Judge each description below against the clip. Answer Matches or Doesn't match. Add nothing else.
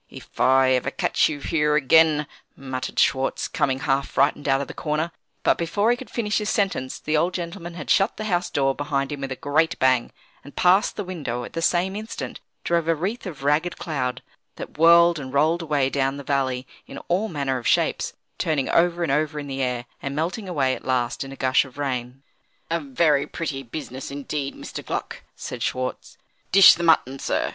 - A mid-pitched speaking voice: Matches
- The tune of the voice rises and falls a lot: Doesn't match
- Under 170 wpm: Doesn't match